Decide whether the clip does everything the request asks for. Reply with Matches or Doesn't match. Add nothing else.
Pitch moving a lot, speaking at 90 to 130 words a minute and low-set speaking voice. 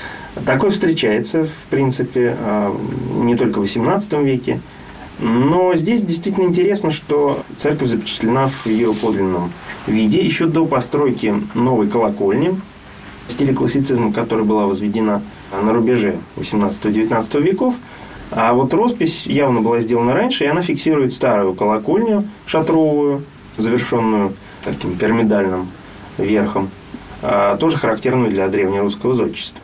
Matches